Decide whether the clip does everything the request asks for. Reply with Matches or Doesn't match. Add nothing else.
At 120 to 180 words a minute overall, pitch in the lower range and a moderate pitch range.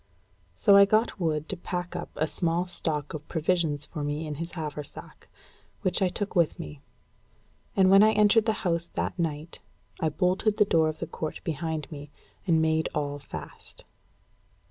Doesn't match